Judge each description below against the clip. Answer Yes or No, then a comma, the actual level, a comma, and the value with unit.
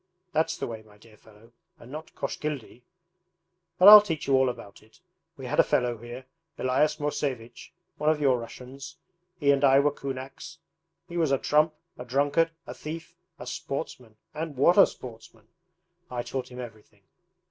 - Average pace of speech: Yes, average, 170 wpm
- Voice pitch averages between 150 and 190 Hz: No, low, 135 Hz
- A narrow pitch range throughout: No, average, 4.1 semitones